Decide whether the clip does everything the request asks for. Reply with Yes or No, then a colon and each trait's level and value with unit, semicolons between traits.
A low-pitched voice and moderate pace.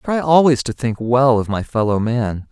No: low, 125 Hz; fast, 240 wpm